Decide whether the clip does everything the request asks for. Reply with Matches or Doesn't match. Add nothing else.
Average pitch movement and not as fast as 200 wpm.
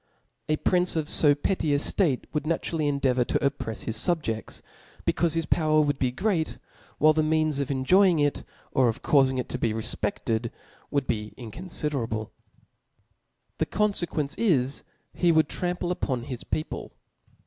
Matches